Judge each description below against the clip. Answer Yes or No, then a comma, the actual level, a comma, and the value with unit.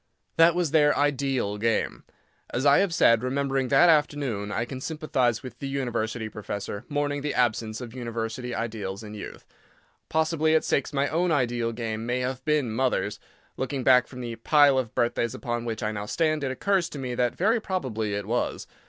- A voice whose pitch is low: Yes, low, 125 Hz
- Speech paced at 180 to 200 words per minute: Yes, average, 190 wpm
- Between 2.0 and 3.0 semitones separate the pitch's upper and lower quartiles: No, average, 4.1 semitones